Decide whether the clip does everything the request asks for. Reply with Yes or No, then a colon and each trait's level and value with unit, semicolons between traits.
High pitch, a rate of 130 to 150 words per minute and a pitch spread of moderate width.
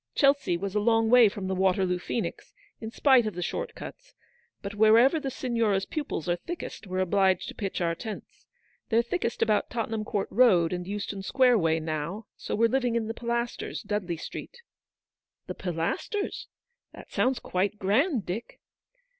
No: high, 215 Hz; average, 170 wpm; average, 4.2 semitones